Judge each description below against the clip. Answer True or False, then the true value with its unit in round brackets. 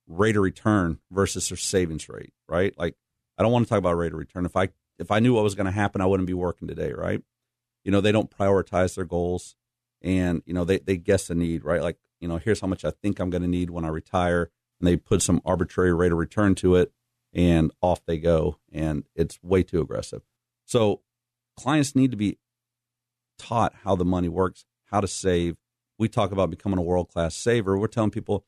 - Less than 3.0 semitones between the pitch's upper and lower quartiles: False (3.6 semitones)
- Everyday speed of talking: False (230 wpm)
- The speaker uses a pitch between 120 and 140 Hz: False (95 Hz)